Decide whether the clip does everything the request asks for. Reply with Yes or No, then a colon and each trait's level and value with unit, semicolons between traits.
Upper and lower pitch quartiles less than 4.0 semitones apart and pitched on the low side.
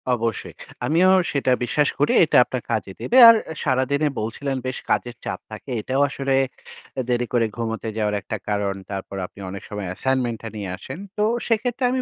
No: average, 4.7 semitones; low, 125 Hz